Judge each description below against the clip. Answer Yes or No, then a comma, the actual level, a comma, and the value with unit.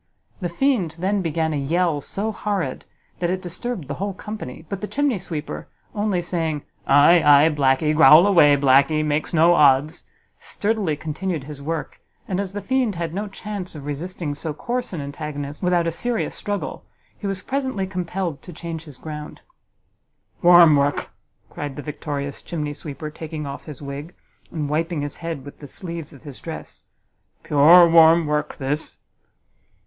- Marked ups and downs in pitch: No, average, 3.9 semitones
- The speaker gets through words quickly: No, average, 165 wpm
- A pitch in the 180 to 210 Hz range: No, medium, 165 Hz